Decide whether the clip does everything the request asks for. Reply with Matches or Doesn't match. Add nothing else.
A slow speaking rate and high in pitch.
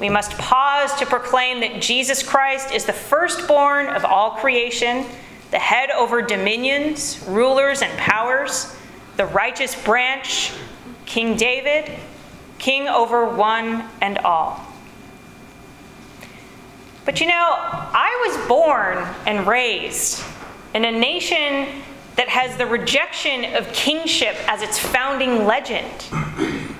Matches